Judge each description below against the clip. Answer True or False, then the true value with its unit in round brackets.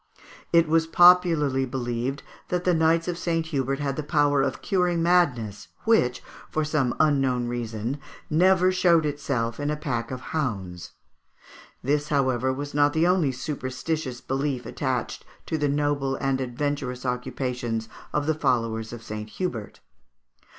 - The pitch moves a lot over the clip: False (4.3 semitones)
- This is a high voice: False (140 Hz)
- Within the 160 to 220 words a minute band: False (145 wpm)